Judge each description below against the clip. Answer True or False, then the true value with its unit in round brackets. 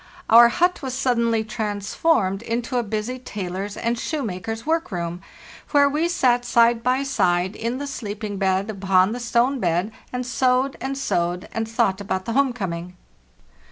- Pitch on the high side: True (230 Hz)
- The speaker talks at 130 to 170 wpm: True (160 wpm)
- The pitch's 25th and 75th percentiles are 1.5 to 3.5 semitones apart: False (4.7 semitones)